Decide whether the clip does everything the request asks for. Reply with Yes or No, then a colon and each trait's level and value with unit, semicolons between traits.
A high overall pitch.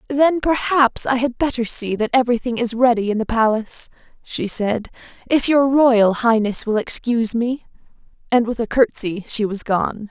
Yes: high, 235 Hz